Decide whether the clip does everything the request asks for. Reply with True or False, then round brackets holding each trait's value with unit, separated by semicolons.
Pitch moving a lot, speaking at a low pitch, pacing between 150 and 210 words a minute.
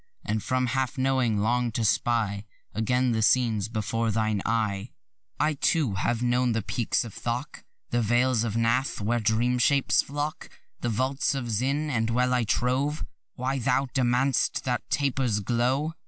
False (2.6 semitones; 120 Hz; 155 wpm)